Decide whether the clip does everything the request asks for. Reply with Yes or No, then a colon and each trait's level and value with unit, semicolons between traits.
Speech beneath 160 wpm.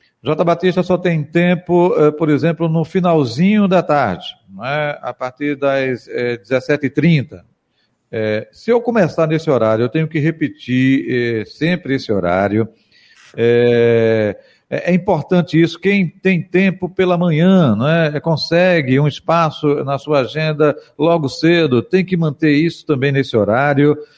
Yes: average, 140 wpm